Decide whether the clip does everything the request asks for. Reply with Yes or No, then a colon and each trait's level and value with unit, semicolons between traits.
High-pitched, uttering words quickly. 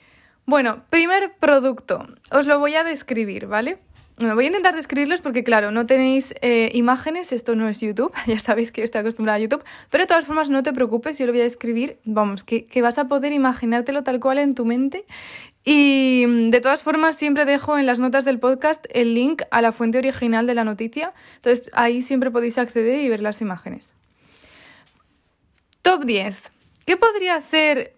Yes: very high, 255 Hz; fast, 195 wpm